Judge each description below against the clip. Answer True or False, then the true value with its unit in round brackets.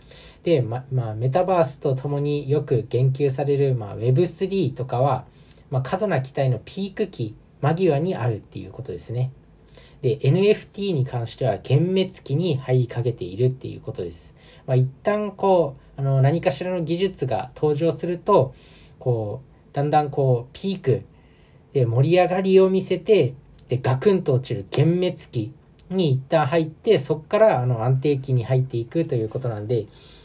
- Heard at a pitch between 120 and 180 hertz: True (140 Hz)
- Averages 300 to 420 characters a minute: True (315 characters per minute)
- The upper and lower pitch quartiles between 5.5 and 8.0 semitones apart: False (5.1 semitones)